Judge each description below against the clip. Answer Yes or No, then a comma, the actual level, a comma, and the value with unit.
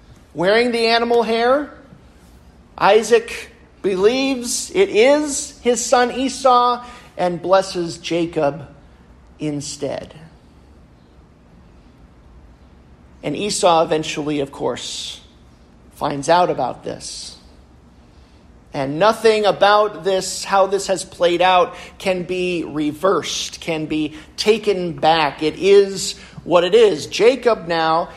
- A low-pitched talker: No, medium, 170 Hz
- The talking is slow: Yes, slow, 100 wpm